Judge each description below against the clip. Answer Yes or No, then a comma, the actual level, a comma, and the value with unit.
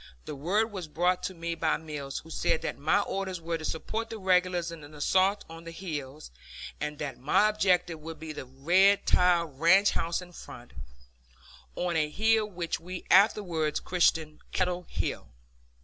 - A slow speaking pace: No, average, 175 wpm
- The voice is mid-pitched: Yes, medium, 170 Hz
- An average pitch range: Yes, average, 3.3 semitones